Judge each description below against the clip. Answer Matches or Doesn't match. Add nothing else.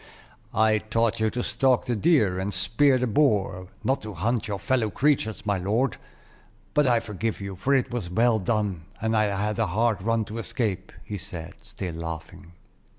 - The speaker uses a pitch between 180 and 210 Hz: Doesn't match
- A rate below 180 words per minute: Doesn't match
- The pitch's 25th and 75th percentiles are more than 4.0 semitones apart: Doesn't match